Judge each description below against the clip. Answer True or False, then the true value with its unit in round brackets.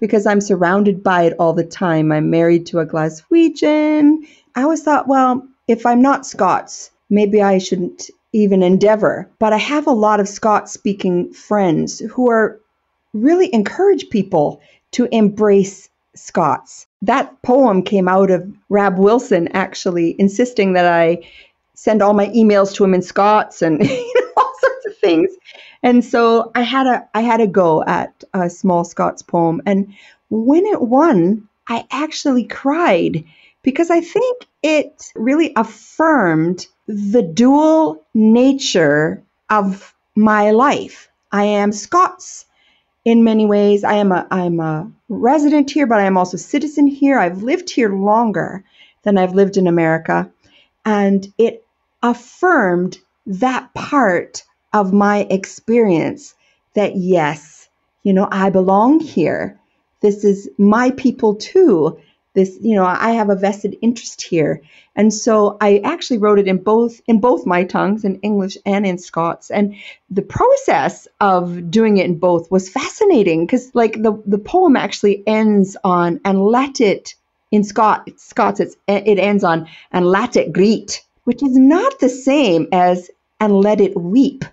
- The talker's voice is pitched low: False (210 Hz)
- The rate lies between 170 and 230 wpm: False (155 wpm)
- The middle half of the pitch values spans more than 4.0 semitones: True (4.9 semitones)